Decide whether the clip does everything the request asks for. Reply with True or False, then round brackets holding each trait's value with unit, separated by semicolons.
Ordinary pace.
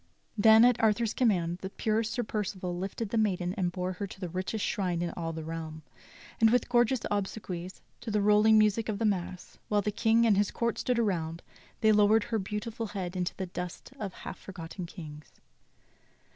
True (195 wpm)